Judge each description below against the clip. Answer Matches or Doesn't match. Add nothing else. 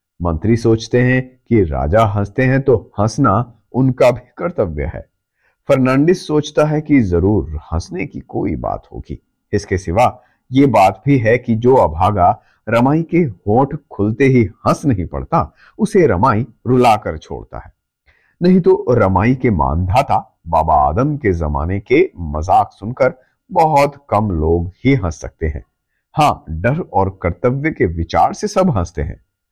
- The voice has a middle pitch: Doesn't match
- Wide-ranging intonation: Matches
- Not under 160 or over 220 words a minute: Doesn't match